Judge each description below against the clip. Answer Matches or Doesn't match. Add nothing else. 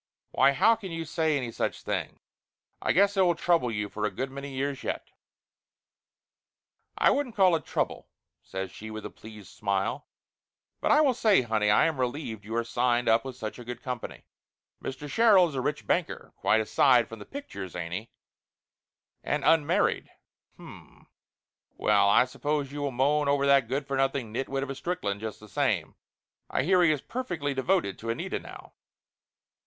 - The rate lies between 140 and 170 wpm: Doesn't match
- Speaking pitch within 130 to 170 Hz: Matches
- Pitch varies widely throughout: Matches